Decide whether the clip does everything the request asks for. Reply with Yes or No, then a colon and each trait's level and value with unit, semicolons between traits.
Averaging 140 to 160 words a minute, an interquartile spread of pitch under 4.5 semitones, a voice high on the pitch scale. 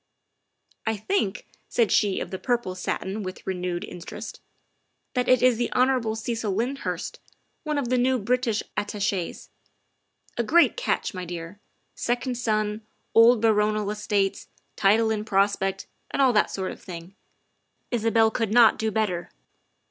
Yes: average, 150 wpm; average, 3.6 semitones; high, 220 Hz